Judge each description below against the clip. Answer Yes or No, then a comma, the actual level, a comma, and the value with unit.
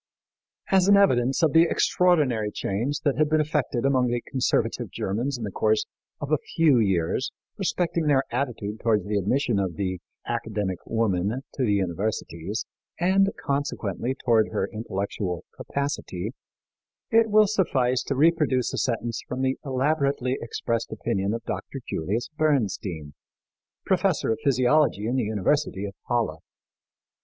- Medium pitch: No, low, 125 Hz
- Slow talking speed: No, average, 145 wpm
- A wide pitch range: Yes, wide, 6.1 semitones